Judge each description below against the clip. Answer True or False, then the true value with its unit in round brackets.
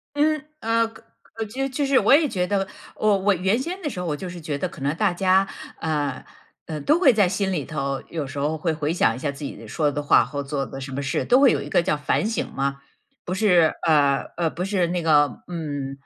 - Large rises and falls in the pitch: True (6.1 semitones)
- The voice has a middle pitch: True (170 Hz)